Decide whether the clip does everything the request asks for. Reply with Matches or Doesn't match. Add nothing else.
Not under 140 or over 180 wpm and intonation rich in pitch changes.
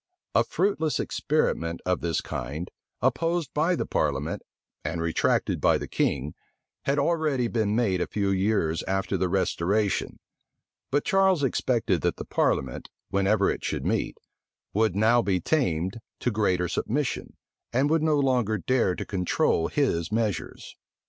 Matches